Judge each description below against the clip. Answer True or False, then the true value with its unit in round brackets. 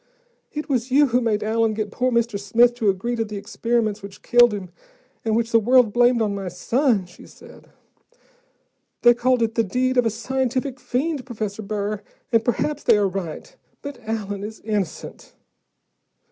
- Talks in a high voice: True (230 Hz)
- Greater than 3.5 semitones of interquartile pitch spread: False (3.2 semitones)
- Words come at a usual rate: True (175 wpm)